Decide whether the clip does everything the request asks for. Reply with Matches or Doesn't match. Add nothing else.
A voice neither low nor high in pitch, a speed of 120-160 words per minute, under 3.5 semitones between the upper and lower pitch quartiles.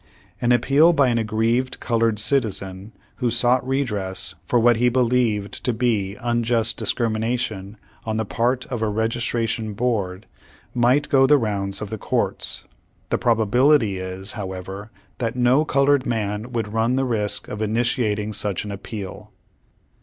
Doesn't match